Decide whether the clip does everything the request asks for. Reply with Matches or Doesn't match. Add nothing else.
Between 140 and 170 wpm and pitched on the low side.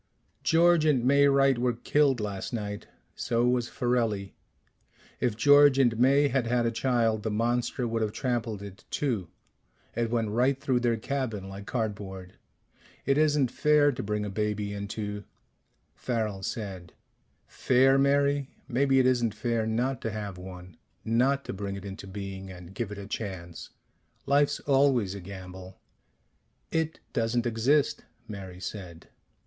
Matches